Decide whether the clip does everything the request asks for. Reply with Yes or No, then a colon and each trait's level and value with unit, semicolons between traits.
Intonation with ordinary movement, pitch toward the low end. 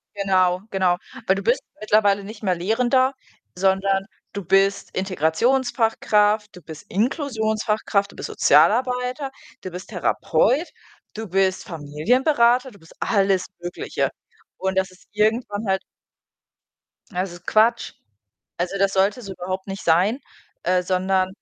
No: average, 3.1 semitones; high, 195 Hz